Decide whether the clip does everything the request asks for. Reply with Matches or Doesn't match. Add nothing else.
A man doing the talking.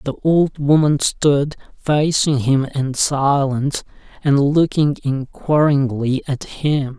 Matches